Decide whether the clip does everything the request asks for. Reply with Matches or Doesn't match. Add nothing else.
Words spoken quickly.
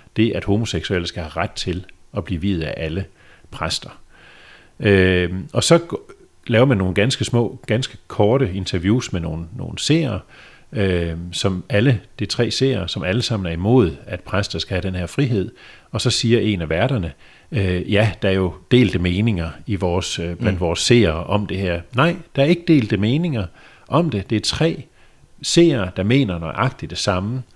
Doesn't match